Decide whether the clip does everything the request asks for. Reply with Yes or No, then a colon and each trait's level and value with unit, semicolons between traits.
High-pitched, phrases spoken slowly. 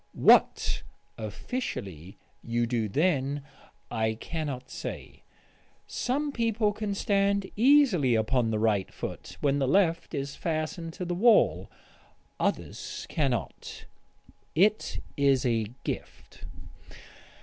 No: medium, 145 Hz; slow, 105 wpm